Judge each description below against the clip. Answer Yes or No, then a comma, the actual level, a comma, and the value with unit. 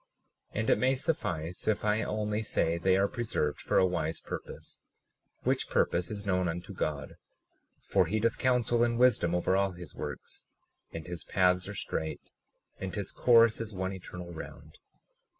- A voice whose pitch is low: Yes, very low, 95 Hz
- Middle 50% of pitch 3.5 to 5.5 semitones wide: Yes, average, 3.9 semitones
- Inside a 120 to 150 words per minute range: No, average, 170 wpm